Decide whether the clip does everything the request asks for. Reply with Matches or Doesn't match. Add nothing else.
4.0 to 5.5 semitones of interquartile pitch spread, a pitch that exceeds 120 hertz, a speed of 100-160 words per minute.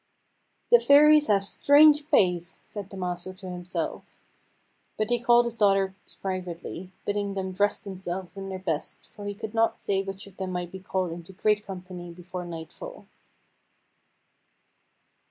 Doesn't match